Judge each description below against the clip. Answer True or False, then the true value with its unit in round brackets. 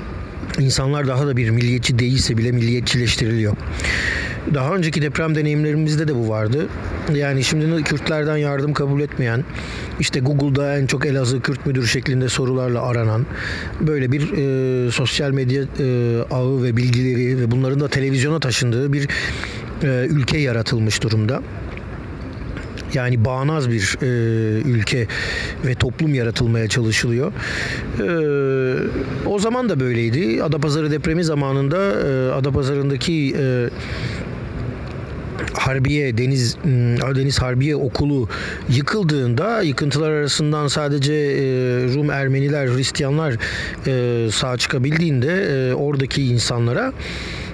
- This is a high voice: False (130 Hz)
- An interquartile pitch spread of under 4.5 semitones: True (3.2 semitones)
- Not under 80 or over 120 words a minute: True (115 wpm)